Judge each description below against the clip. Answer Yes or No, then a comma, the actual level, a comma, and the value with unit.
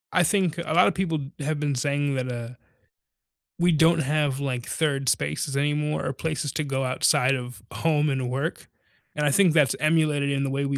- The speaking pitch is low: No, medium, 145 Hz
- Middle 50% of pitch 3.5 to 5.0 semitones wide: No, narrow, 2.6 semitones